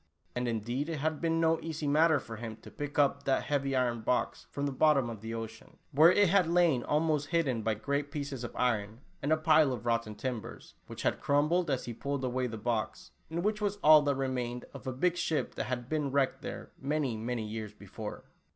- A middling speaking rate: No, fast, 235 wpm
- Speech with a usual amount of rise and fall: Yes, average, 4.5 semitones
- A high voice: No, low, 135 Hz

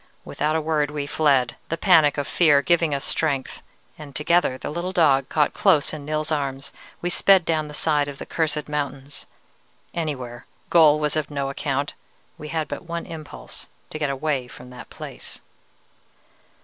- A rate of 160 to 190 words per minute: Yes, average, 175 wpm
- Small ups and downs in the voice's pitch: Yes, narrow, 2.2 semitones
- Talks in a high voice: No, medium, 150 Hz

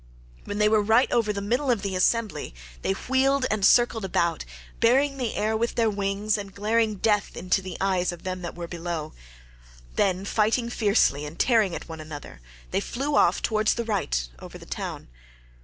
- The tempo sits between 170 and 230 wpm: Yes, average, 190 wpm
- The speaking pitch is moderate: No, high, 205 Hz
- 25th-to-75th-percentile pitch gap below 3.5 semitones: No, average, 4.0 semitones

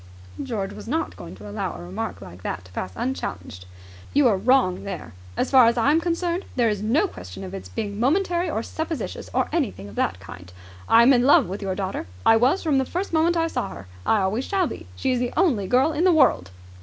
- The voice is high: Yes, high, 235 Hz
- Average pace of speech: No, fast, 235 wpm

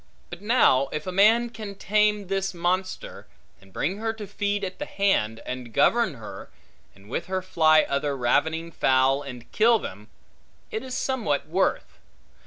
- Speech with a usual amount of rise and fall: No, wide, 7.1 semitones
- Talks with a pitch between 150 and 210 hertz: Yes, medium, 185 Hz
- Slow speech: No, average, 165 wpm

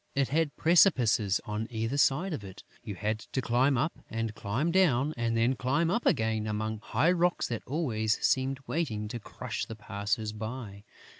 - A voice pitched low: Yes, low, 120 Hz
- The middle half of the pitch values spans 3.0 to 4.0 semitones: No, average, 4.7 semitones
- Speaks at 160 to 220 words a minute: Yes, average, 175 wpm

